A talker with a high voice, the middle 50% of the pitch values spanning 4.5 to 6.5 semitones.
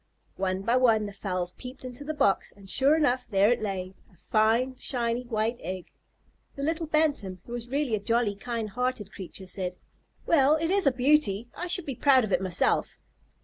Yes: high, 235 Hz; wide, 5.5 semitones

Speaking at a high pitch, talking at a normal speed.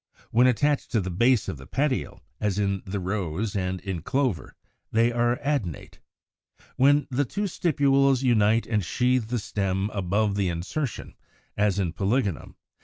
No: low, 110 Hz; average, 170 wpm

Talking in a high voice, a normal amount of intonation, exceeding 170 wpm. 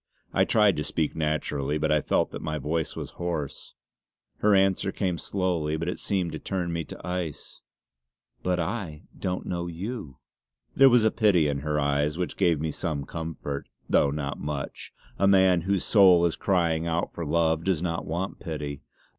No: very low, 85 Hz; average, 3.4 semitones; average, 180 wpm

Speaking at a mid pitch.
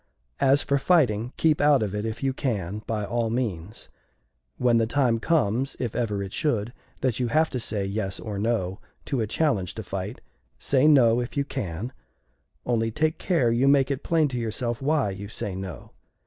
No: low, 115 Hz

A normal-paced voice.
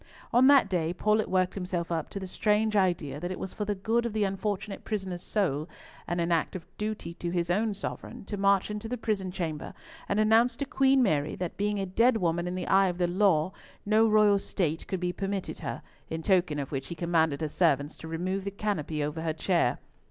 No: fast, 225 wpm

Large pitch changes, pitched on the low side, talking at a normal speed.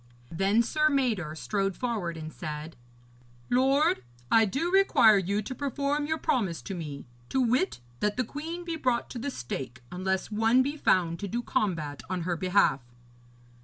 No: wide, 7.5 semitones; high, 215 Hz; average, 165 wpm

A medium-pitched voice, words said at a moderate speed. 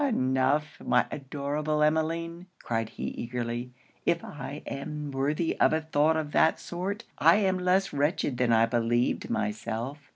Yes: medium, 145 Hz; average, 150 wpm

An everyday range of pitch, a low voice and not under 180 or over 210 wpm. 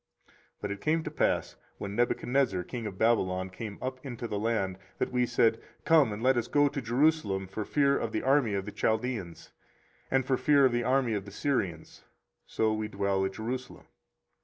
Yes: average, 4.6 semitones; low, 115 Hz; average, 200 wpm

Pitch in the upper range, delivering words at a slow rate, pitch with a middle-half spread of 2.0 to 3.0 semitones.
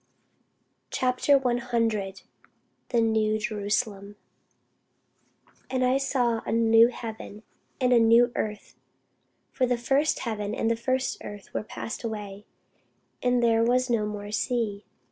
Yes: high, 230 Hz; slow, 125 wpm; average, 2.7 semitones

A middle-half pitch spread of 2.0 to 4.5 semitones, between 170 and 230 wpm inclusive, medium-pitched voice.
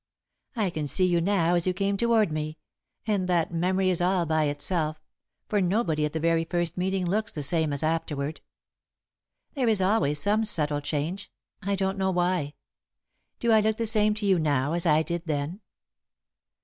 Yes: average, 4.2 semitones; average, 185 wpm; medium, 175 Hz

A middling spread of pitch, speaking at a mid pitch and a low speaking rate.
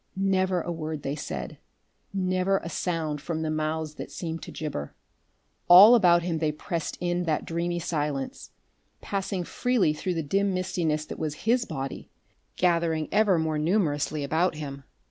No: average, 3.1 semitones; medium, 165 Hz; average, 160 wpm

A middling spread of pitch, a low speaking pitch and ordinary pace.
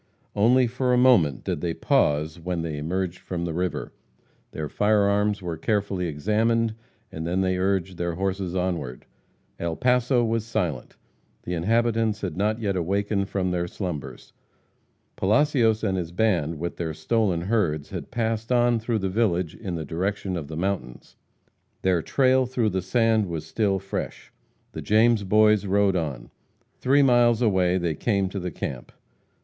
Yes: average, 4.4 semitones; very low, 95 Hz; average, 165 wpm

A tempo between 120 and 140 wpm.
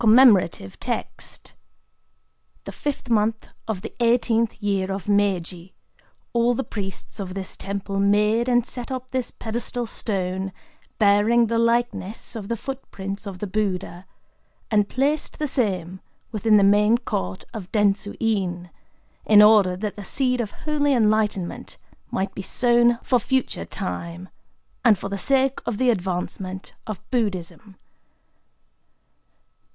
Yes: slow, 135 wpm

